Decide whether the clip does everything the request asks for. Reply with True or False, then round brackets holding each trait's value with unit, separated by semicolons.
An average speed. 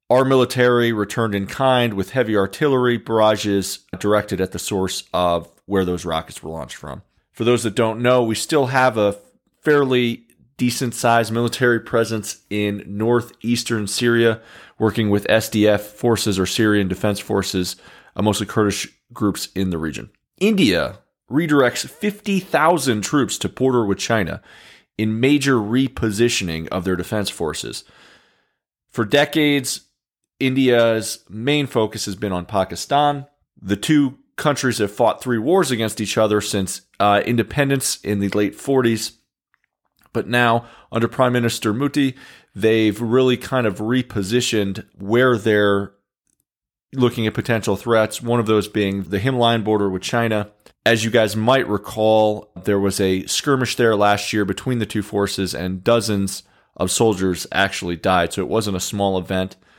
True (145 wpm)